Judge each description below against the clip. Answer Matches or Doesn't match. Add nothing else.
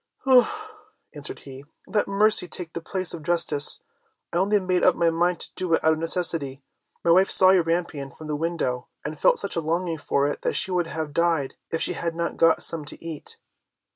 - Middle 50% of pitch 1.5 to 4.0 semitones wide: Matches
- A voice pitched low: Doesn't match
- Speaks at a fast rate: Matches